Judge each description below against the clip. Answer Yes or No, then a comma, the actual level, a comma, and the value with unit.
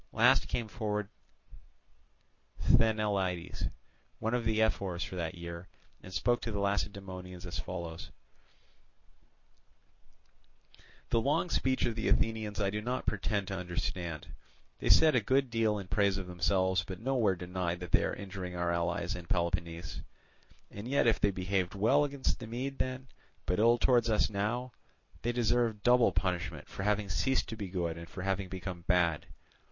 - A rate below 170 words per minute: Yes, average, 160 wpm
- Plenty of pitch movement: No, average, 4.1 semitones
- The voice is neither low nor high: No, low, 100 Hz